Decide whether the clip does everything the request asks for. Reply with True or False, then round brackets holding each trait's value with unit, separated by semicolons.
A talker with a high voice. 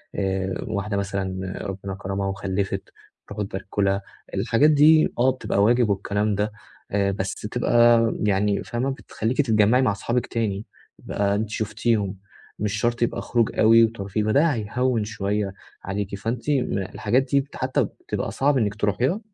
False (105 Hz)